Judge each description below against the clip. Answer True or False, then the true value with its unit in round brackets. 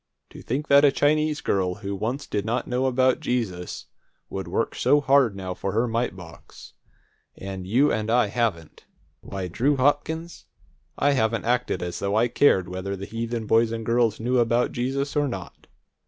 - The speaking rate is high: False (180 wpm)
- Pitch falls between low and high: False (115 Hz)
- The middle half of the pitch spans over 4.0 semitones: True (5.1 semitones)